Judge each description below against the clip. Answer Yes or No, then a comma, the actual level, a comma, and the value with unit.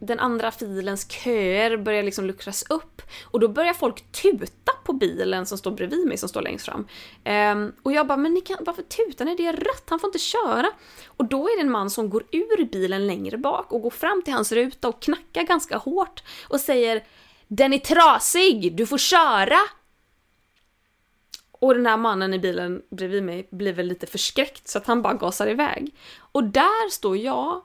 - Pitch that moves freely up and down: Yes, wide, 8.3 semitones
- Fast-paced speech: Yes, fast, 200 wpm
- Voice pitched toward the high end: Yes, very high, 260 Hz